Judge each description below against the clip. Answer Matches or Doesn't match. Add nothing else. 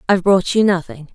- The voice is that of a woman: Matches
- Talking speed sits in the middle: Doesn't match